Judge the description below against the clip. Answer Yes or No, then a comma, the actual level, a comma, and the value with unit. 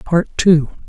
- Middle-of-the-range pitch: Yes, medium, 160 Hz